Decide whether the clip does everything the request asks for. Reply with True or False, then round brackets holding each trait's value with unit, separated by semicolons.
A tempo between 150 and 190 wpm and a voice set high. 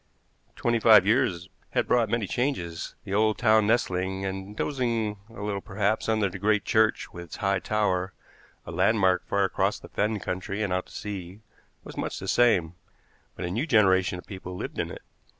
False (185 wpm; 100 Hz)